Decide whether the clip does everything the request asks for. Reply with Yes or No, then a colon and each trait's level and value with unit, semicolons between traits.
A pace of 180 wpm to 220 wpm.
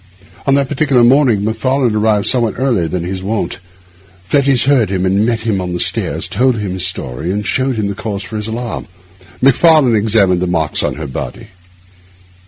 Yes: average, 190 wpm